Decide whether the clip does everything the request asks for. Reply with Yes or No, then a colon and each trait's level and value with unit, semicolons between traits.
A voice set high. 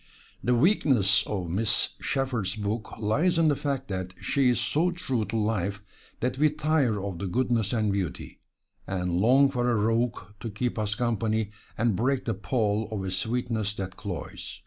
No: low, 110 Hz